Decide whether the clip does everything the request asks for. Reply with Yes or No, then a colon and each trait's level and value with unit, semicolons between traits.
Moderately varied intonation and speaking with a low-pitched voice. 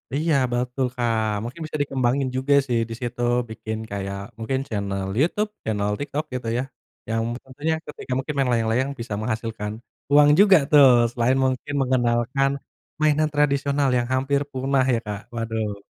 Yes: average, 3.7 semitones; low, 130 Hz